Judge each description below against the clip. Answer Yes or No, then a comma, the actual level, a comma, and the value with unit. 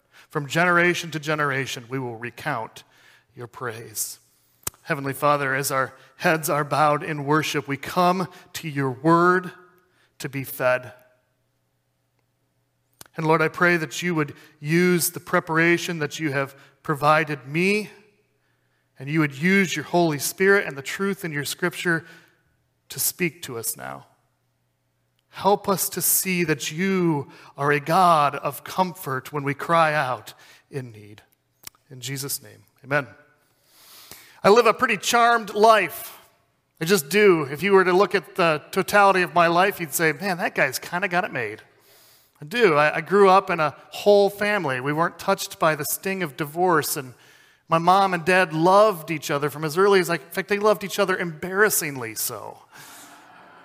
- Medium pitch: Yes, medium, 160 Hz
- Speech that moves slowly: No, average, 165 wpm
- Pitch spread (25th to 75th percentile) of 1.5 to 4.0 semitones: No, average, 4.7 semitones